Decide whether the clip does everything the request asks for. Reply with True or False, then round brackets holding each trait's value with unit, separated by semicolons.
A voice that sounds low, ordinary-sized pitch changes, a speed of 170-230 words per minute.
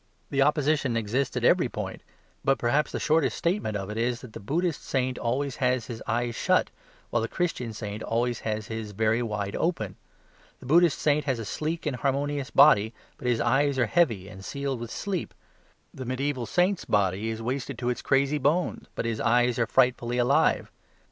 True (125 Hz; 4.0 semitones; 190 wpm)